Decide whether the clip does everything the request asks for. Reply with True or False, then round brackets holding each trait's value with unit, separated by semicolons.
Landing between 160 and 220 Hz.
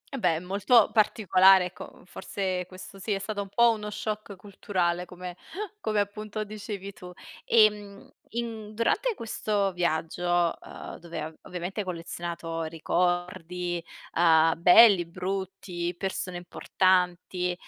True (185 Hz)